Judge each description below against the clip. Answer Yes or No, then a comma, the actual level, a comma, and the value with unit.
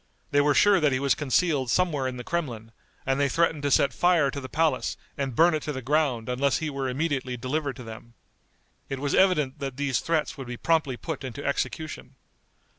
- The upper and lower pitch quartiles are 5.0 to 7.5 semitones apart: No, average, 3.2 semitones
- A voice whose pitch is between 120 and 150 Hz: Yes, medium, 140 Hz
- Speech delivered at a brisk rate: Yes, fast, 210 wpm